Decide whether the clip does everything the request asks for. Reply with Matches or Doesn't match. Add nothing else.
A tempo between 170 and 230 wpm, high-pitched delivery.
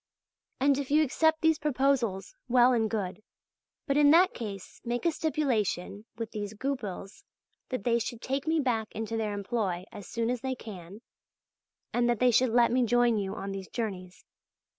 Matches